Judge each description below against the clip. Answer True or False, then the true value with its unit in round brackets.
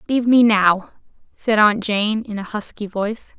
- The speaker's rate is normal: True (175 wpm)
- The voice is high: True (215 Hz)